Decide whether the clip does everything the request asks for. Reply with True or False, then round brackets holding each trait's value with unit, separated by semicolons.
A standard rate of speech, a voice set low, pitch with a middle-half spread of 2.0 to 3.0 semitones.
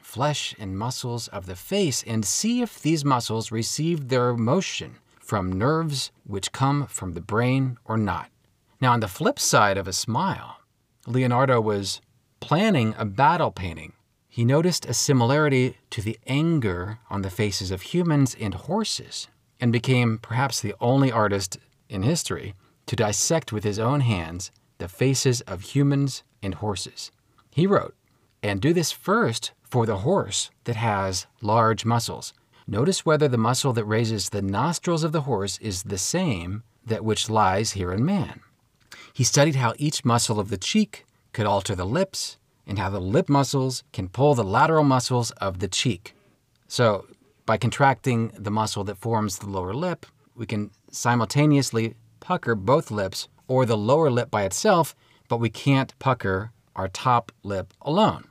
False (165 wpm; 115 Hz; 4.6 semitones)